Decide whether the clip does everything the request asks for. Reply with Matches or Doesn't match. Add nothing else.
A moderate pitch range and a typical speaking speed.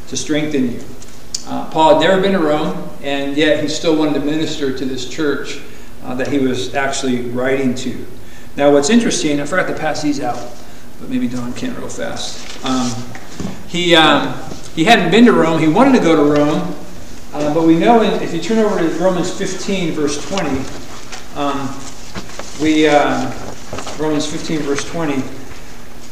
Matches